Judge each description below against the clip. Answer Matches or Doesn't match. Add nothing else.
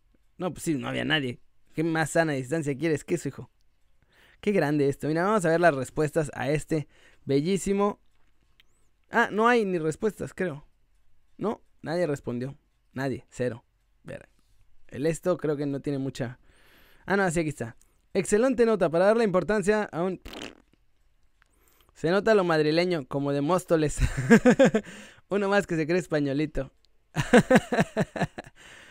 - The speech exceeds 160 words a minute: Doesn't match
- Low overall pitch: Doesn't match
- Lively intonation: Matches